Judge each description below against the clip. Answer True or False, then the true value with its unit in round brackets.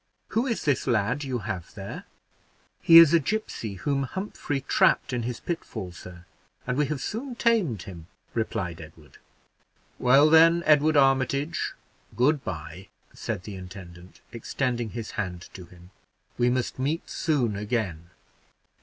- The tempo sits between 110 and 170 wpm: True (145 wpm)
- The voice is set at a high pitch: False (125 Hz)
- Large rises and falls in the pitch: True (7.8 semitones)